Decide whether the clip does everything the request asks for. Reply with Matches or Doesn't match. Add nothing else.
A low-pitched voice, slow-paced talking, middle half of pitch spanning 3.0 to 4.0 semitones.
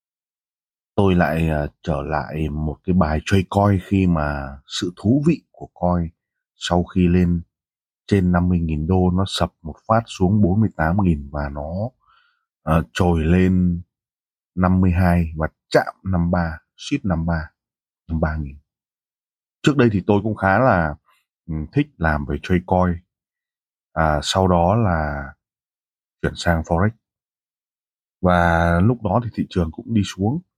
Matches